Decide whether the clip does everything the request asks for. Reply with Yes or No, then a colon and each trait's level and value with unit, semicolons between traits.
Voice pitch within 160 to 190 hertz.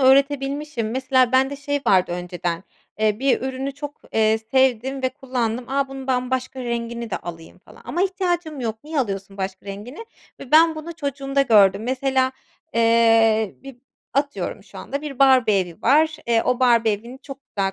No: very high, 255 Hz